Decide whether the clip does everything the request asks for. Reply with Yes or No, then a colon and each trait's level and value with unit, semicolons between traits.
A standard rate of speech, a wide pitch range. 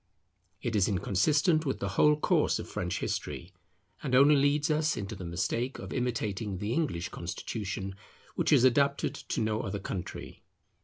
Yes: average, 160 wpm; wide, 6.4 semitones